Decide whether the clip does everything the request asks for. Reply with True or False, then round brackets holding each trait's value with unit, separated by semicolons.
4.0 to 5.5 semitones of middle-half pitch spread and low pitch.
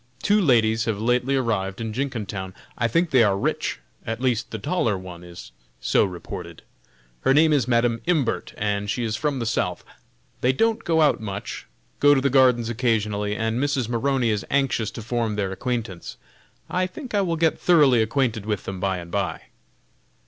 True (4.8 semitones; 115 Hz)